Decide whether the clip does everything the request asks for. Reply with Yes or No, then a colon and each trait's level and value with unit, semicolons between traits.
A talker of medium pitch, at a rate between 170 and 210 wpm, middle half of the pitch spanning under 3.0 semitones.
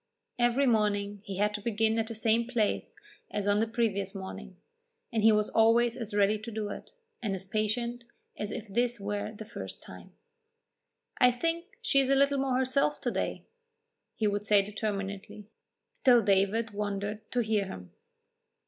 No: high, 215 Hz; average, 175 wpm; narrow, 2.6 semitones